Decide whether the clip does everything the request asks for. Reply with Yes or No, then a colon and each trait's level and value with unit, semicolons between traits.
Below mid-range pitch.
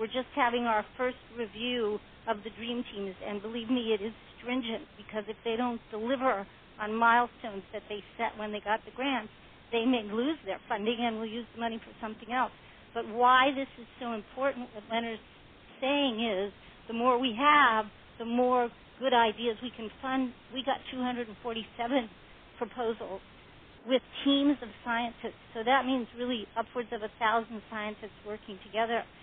No: high, 230 Hz